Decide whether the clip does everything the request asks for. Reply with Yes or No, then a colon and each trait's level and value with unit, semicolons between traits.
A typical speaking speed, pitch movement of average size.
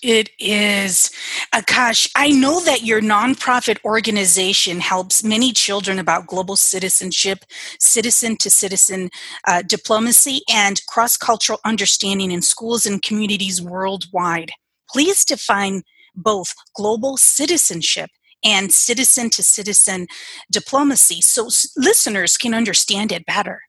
No: slow, 115 wpm; average, 3.5 semitones